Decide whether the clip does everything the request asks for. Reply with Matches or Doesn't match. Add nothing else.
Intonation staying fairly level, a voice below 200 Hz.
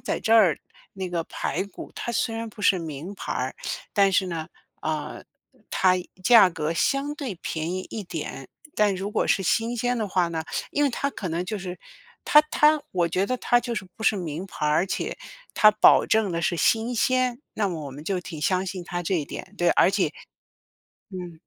Doesn't match